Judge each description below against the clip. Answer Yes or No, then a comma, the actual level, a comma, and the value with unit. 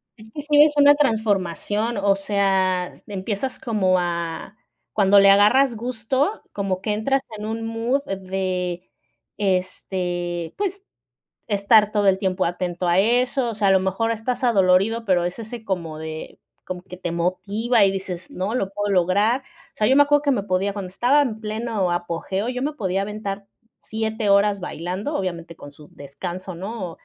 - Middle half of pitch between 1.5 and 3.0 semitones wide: No, average, 3.6 semitones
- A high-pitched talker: Yes, high, 200 Hz